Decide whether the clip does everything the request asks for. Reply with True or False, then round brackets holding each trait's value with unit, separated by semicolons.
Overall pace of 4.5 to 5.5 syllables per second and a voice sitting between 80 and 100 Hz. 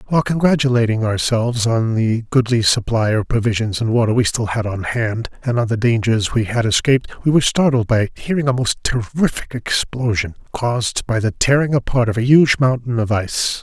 False (5.4 syllables/s; 120 Hz)